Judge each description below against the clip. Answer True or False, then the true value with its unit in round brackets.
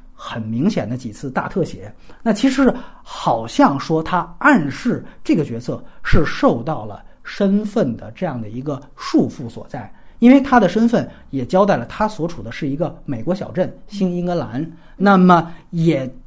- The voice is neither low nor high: True (175 Hz)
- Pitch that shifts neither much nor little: False (6.4 semitones)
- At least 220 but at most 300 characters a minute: True (245 characters per minute)